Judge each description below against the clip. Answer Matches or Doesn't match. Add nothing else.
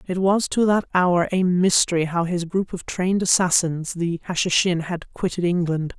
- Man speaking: Doesn't match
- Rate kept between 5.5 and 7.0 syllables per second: Doesn't match